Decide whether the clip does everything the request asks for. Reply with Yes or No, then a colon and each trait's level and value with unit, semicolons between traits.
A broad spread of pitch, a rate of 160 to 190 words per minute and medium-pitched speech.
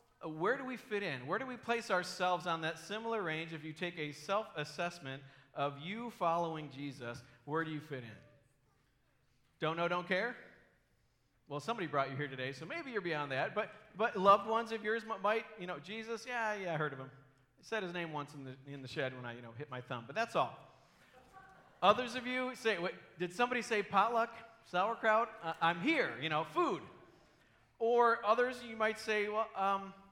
No: wide, 7.3 semitones; fast, 205 wpm; medium, 180 Hz